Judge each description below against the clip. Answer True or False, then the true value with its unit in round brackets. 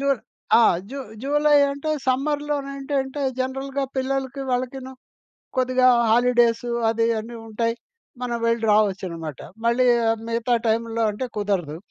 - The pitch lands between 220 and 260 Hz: True (250 Hz)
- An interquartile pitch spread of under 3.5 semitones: True (3.1 semitones)